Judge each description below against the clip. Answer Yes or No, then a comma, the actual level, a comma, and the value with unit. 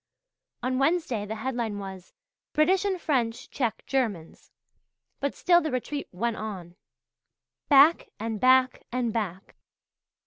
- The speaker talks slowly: Yes, slow, 125 wpm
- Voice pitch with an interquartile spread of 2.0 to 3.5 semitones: No, average, 4.8 semitones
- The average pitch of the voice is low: No, high, 245 Hz